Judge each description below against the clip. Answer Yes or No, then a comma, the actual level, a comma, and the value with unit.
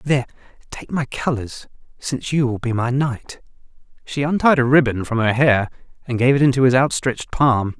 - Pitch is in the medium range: No, low, 130 Hz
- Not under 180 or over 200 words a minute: Yes, average, 190 wpm